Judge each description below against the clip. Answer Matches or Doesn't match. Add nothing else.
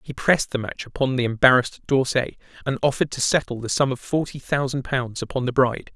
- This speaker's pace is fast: Matches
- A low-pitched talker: Matches